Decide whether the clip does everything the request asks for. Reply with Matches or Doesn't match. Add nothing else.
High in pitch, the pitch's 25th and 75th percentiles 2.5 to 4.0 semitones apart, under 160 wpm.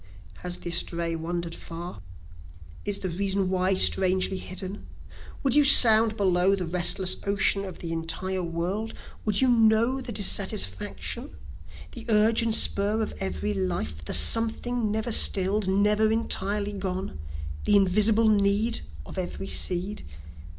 Matches